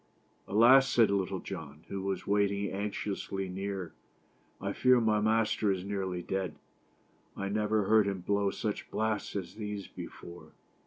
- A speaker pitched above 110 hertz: No, low, 100 Hz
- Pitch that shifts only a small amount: Yes, narrow, 1.8 semitones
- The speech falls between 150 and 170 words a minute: Yes, average, 155 wpm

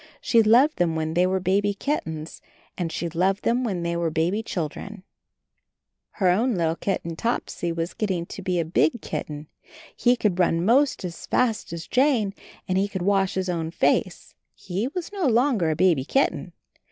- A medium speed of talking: Yes, average, 175 wpm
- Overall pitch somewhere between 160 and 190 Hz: Yes, medium, 185 Hz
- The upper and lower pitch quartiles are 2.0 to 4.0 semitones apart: No, average, 5.0 semitones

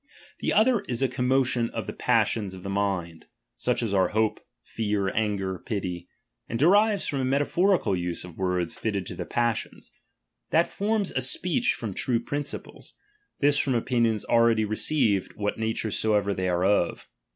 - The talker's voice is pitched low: Yes, low, 110 Hz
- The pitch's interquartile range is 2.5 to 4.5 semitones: No, average, 5.3 semitones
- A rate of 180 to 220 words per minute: Yes, average, 185 wpm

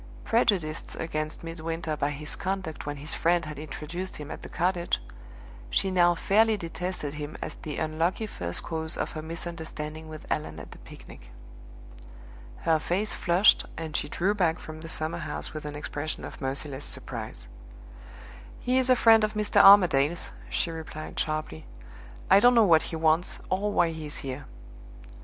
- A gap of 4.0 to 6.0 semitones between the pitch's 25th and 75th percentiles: No, average, 3.2 semitones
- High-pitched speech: No, medium, 160 Hz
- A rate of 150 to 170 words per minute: Yes, average, 165 wpm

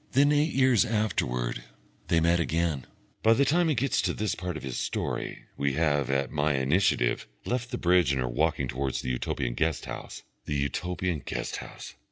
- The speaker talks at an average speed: Yes, average, 190 wpm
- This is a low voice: Yes, very low, 80 Hz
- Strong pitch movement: Yes, wide, 8.1 semitones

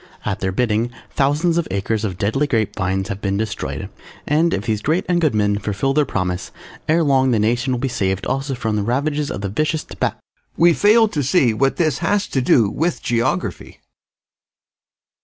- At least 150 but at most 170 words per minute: No, average, 195 wpm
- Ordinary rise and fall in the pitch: No, wide, 6.4 semitones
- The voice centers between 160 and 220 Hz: No, low, 125 Hz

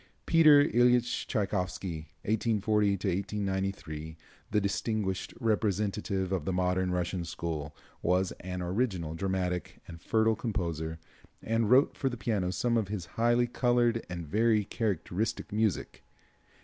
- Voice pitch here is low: Yes, low, 100 Hz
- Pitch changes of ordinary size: Yes, average, 3.9 semitones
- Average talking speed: No, slow, 125 wpm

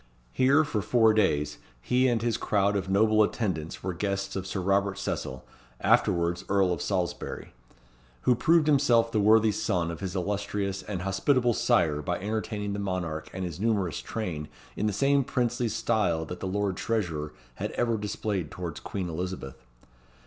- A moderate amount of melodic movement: Yes, average, 3.8 semitones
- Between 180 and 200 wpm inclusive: No, average, 165 wpm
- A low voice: Yes, low, 100 Hz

